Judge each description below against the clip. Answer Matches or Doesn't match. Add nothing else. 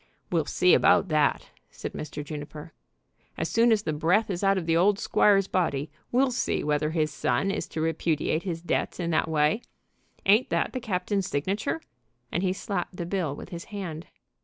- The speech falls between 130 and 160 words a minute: Doesn't match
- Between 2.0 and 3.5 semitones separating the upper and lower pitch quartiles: Doesn't match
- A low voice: Doesn't match